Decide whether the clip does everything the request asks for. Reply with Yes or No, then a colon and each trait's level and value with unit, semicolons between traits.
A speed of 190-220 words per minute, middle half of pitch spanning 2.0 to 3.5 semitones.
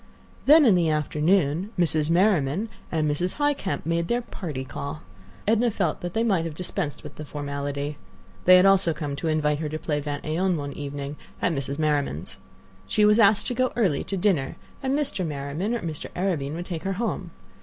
No: average, 200 wpm; average, 4.9 semitones